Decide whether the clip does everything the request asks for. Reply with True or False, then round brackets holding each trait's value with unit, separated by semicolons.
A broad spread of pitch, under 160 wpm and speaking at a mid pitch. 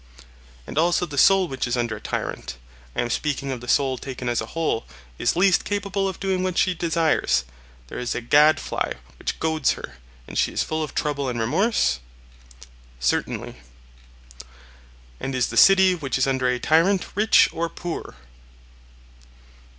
False (6.2 semitones; 165 wpm; 150 Hz)